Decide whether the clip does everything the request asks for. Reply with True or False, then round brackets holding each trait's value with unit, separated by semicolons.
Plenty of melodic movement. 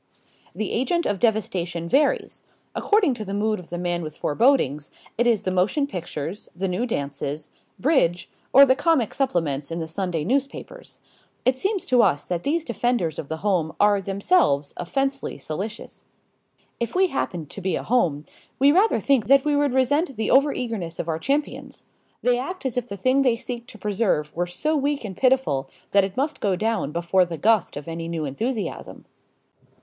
True (7.7 semitones)